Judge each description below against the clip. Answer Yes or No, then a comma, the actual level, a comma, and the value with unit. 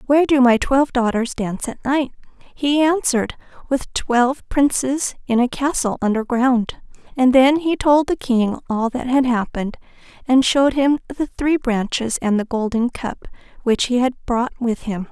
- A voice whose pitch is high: Yes, very high, 255 Hz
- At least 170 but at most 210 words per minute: Yes, average, 175 wpm